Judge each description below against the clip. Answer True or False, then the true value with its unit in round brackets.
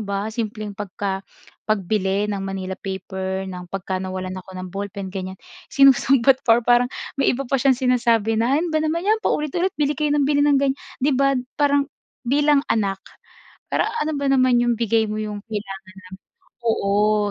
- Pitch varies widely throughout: True (5.8 semitones)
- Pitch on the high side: True (225 Hz)